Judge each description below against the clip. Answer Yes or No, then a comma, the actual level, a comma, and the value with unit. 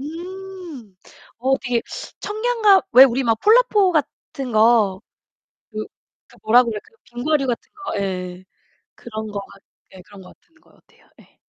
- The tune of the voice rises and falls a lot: Yes, wide, 8.2 semitones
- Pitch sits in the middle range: No, high, 245 Hz